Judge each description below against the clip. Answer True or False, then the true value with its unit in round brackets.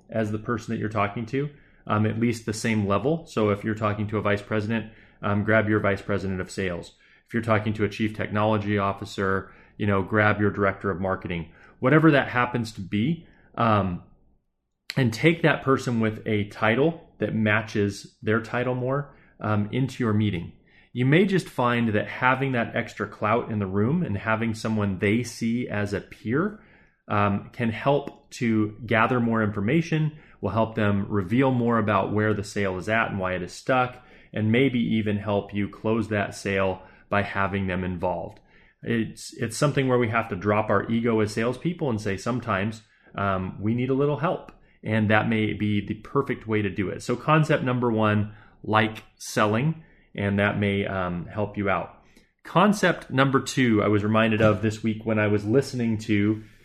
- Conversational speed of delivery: True (190 wpm)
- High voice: False (110 Hz)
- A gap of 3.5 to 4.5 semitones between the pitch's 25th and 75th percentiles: False (2.9 semitones)